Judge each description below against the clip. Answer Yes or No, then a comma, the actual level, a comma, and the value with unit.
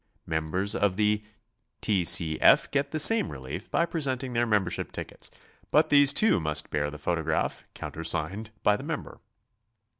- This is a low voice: Yes, low, 105 Hz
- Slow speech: No, average, 160 wpm